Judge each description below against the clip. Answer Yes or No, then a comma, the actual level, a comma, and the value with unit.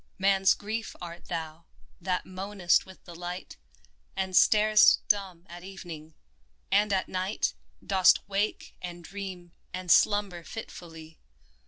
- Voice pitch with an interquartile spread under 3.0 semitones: Yes, narrow, 2.4 semitones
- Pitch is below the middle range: No, medium, 185 Hz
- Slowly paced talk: Yes, slow, 130 wpm